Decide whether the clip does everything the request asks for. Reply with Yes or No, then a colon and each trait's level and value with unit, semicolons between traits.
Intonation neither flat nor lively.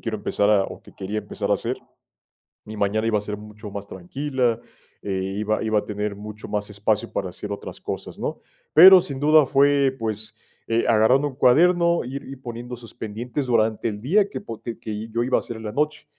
Yes: average, 4.2 semitones